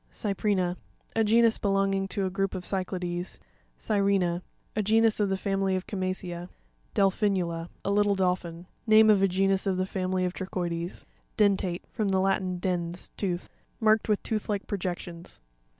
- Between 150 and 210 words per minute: Yes, average, 155 wpm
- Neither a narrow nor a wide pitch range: No, narrow, 1.9 semitones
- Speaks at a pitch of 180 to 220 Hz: Yes, high, 190 Hz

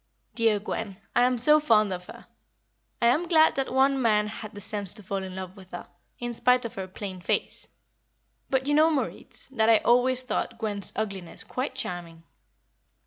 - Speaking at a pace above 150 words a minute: Yes, average, 190 wpm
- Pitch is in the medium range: No, high, 220 Hz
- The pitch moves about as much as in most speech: Yes, average, 4.7 semitones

